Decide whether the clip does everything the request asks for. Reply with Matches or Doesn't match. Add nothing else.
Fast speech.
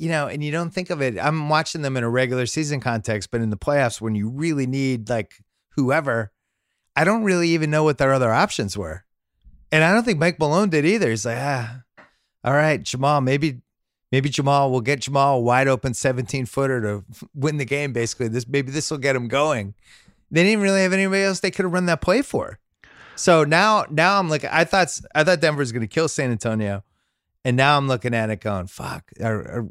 Matches